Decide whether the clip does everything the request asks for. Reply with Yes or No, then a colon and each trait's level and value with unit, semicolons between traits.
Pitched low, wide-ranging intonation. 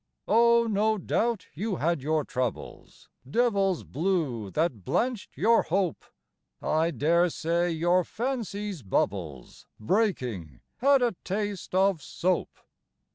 No: medium, 180 Hz; wide, 6.0 semitones